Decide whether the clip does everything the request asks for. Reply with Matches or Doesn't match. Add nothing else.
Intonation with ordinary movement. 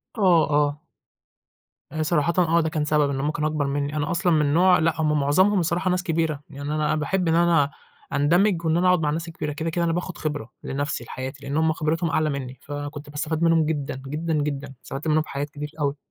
Doesn't match